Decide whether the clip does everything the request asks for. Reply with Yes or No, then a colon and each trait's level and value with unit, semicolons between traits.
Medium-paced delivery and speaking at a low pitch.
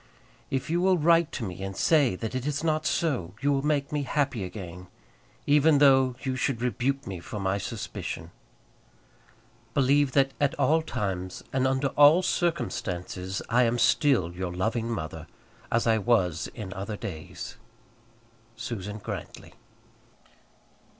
Yes: average, 145 wpm; low, 125 Hz